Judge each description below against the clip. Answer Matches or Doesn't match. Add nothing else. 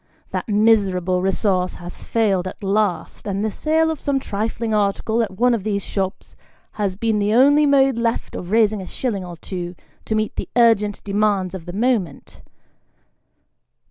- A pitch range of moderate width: Matches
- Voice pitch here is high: Matches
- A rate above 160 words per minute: Matches